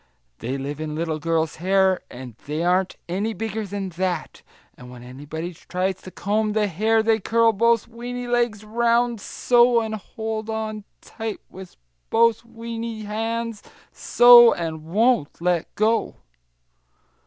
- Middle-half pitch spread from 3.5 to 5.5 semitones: Yes, average, 4.9 semitones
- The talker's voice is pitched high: Yes, high, 215 Hz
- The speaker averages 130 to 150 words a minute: Yes, average, 145 wpm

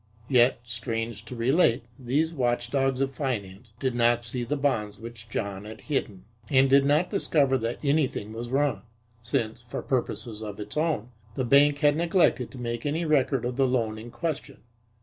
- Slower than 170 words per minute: No, average, 175 wpm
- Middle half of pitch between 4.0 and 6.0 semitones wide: No, average, 3.4 semitones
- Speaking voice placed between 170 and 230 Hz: No, low, 125 Hz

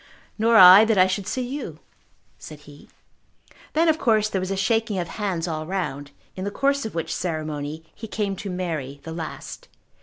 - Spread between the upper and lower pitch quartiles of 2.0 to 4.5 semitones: No, average, 5.2 semitones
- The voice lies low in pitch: No, medium, 185 Hz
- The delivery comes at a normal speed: Yes, average, 190 wpm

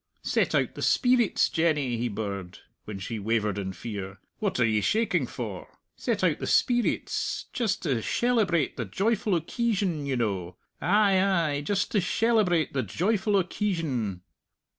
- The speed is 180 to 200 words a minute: No, average, 150 wpm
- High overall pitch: No, medium, 160 Hz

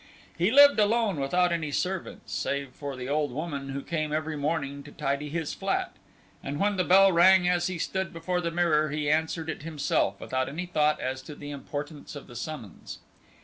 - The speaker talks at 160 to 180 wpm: No, average, 195 wpm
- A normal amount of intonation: Yes, average, 3.7 semitones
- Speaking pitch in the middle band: Yes, medium, 155 Hz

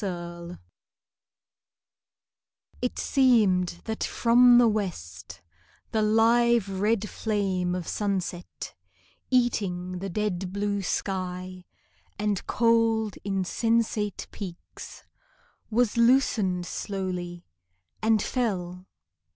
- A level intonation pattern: No, average, 3.8 semitones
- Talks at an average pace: No, slow, 85 wpm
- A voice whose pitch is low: No, high, 200 Hz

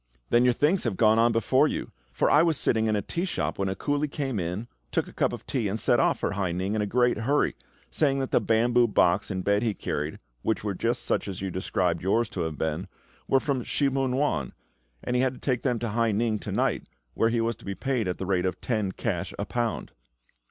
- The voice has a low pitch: Yes, low, 115 Hz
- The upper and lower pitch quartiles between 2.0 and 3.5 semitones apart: No, average, 4.5 semitones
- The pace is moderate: No, fast, 250 wpm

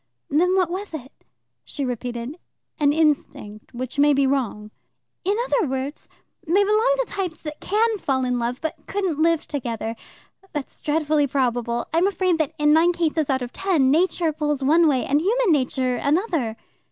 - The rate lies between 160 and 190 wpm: Yes, average, 170 wpm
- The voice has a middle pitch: No, very high, 300 Hz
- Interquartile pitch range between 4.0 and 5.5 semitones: Yes, average, 5.1 semitones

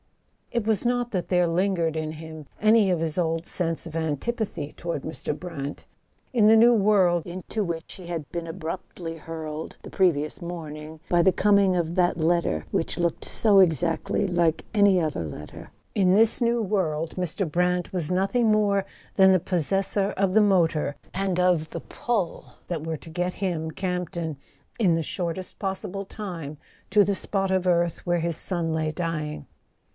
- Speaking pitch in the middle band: Yes, medium, 175 Hz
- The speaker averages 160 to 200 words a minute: Yes, average, 170 wpm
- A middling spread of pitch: Yes, average, 3.2 semitones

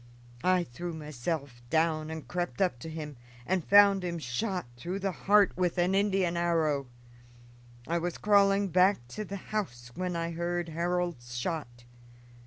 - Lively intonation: No, average, 3.4 semitones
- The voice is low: No, medium, 175 Hz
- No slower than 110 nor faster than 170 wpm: Yes, average, 155 wpm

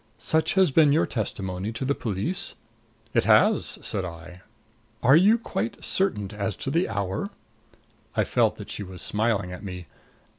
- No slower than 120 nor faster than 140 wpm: No, average, 160 wpm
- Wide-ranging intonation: Yes, wide, 8.1 semitones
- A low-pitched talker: Yes, low, 105 Hz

